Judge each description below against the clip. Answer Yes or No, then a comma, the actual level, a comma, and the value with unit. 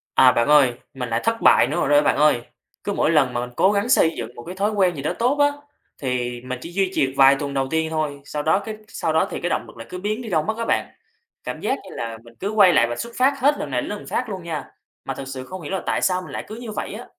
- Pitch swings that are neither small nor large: No, wide, 7.4 semitones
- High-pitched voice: No, medium, 160 Hz